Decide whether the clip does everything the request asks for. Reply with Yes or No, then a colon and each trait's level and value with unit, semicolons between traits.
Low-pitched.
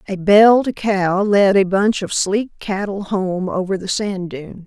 No: high, 195 Hz